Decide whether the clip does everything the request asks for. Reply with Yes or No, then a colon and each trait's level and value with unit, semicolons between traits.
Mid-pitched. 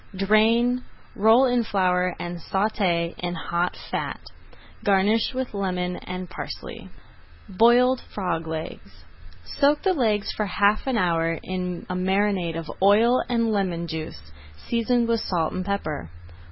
No: high, 195 Hz